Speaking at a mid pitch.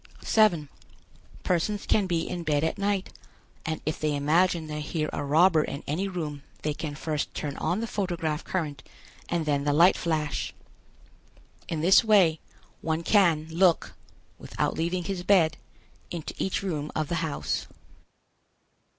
Yes: medium, 165 Hz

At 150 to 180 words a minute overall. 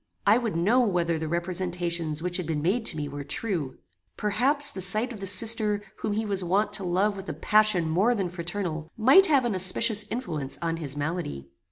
No: fast, 205 wpm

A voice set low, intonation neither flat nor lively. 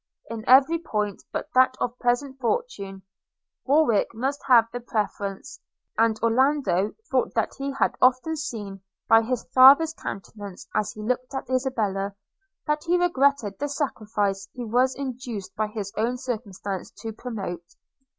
No: high, 240 Hz; average, 4.3 semitones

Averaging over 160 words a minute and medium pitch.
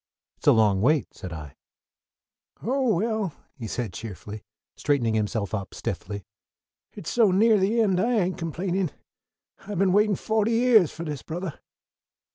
No: average, 150 wpm; medium, 175 Hz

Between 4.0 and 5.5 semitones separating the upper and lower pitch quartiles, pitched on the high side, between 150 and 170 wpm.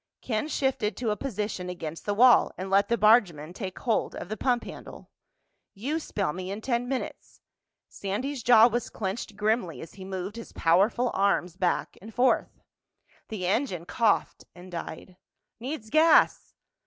Yes: average, 4.4 semitones; high, 210 Hz; average, 160 wpm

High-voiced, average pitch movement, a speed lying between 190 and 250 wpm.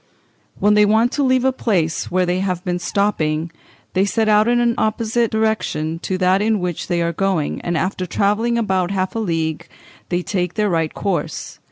Yes: high, 195 Hz; average, 3.7 semitones; average, 195 wpm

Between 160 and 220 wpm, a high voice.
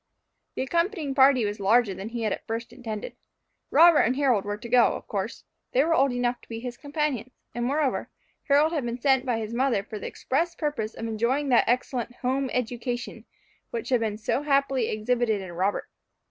Yes: average, 200 wpm; high, 245 Hz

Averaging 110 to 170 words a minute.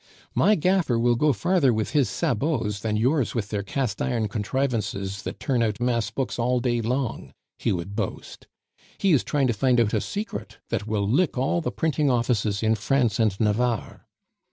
No: average, 185 wpm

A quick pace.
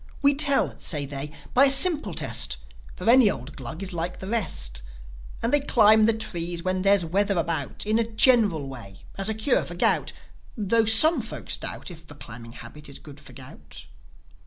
No: average, 190 wpm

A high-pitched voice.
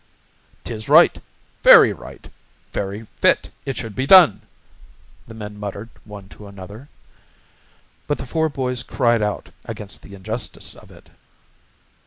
No: low, 110 Hz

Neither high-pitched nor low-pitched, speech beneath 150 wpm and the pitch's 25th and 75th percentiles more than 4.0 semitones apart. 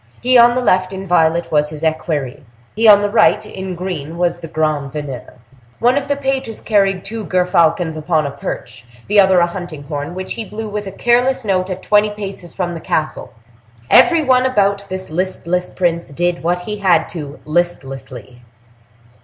No: medium, 180 Hz; average, 185 wpm; average, 4.6 semitones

